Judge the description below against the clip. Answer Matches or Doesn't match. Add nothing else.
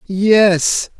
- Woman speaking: Doesn't match